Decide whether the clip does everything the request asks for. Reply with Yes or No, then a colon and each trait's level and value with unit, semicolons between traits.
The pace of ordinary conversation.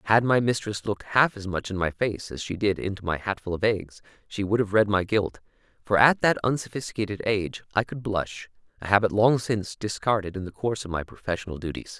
No: fast, 220 wpm